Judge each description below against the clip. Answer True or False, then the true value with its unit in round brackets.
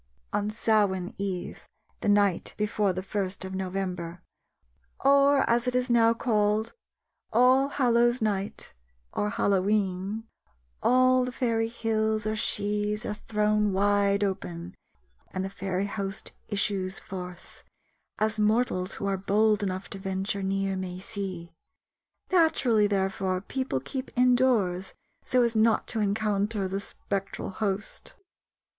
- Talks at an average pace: False (125 wpm)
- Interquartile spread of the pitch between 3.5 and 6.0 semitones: False (2.7 semitones)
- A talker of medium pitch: False (205 Hz)